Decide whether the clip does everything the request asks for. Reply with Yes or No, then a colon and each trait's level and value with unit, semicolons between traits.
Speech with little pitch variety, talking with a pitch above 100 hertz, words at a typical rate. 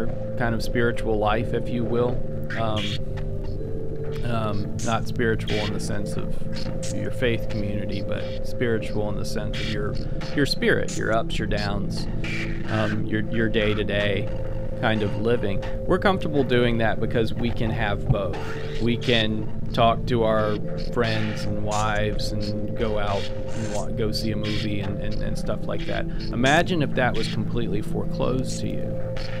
Yes: narrow, 1.6 semitones; low, 110 Hz; average, 160 wpm